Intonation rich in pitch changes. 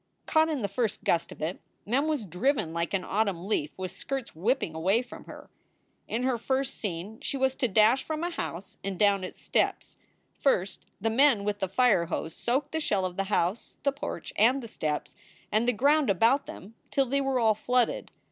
Yes: wide, 5.9 semitones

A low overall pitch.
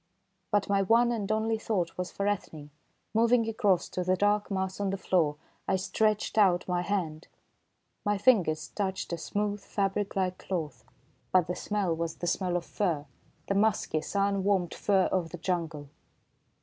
No: high, 190 Hz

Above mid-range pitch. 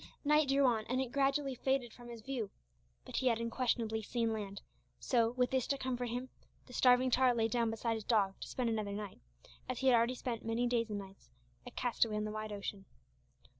Yes: high, 235 Hz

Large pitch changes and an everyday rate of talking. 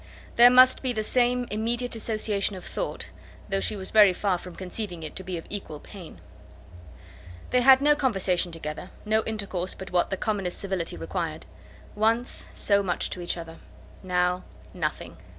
No: average, 4.0 semitones; average, 170 wpm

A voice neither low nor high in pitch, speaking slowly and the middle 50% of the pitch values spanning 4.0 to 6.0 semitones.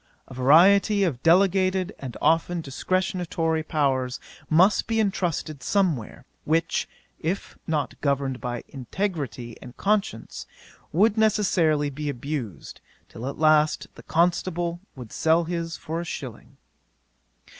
Yes: medium, 160 Hz; slow, 120 wpm; average, 5.0 semitones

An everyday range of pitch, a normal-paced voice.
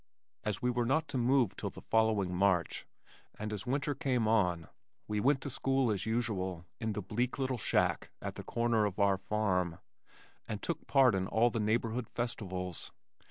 Yes: average, 3.9 semitones; average, 180 wpm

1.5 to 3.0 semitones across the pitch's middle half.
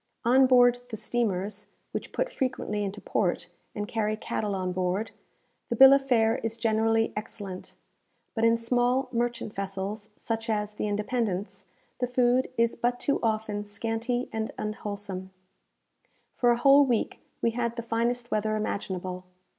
Yes: average, 2.7 semitones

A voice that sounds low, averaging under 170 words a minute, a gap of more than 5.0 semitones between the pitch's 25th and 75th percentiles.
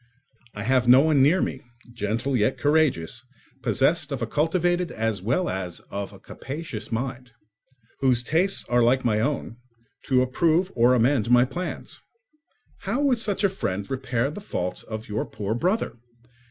Yes: low, 130 Hz; average, 160 wpm; wide, 5.6 semitones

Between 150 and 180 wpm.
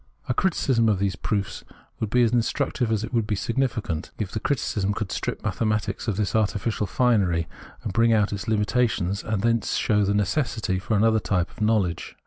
No: average, 190 wpm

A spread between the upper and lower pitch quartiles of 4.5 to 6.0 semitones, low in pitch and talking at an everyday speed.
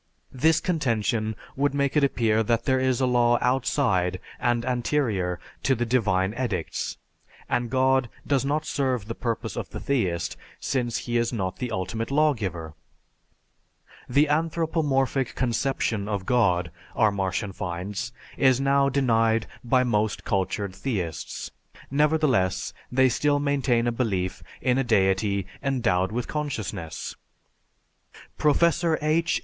No: average, 5.0 semitones; low, 120 Hz; slow, 130 wpm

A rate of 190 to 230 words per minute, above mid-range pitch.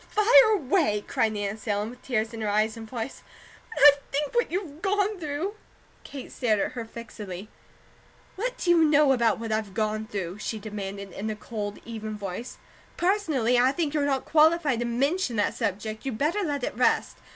Yes: average, 195 wpm; high, 240 Hz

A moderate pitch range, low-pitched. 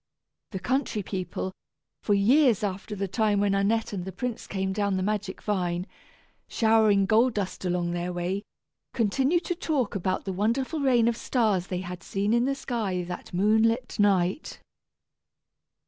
No: average, 3.7 semitones; high, 205 Hz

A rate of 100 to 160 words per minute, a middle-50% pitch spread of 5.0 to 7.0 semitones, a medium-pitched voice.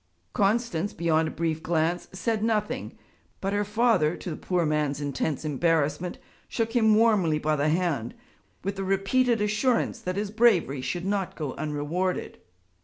Yes: average, 155 wpm; average, 5.3 semitones; medium, 180 Hz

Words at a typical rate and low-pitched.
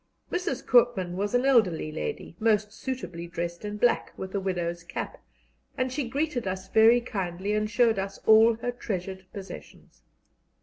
No: average, 160 wpm; high, 210 Hz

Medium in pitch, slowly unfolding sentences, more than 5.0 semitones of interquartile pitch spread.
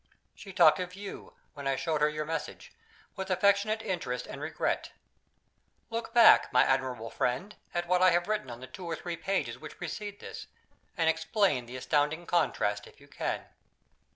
No: medium, 165 Hz; average, 180 wpm; wide, 5.5 semitones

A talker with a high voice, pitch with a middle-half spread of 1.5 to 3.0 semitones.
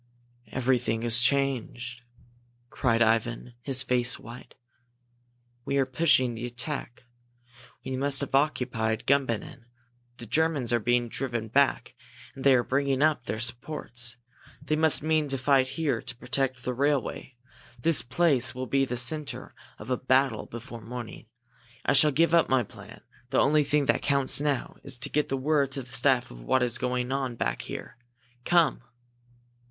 No: low, 130 Hz; average, 2.7 semitones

